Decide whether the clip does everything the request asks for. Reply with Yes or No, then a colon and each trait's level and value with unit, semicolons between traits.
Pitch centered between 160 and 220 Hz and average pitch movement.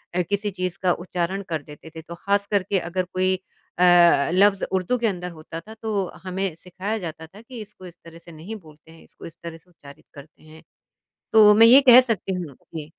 Yes: medium, 185 Hz; average, 3.7 semitones